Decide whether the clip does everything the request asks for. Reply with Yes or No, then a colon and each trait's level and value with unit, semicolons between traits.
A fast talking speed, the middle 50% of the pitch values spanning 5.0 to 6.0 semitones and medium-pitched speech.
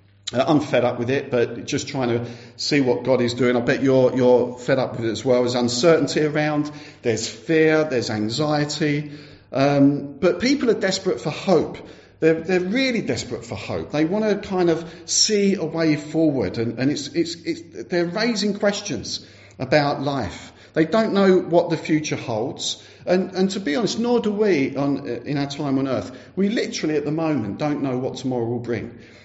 No: average, 195 wpm; wide, 5.6 semitones; medium, 145 Hz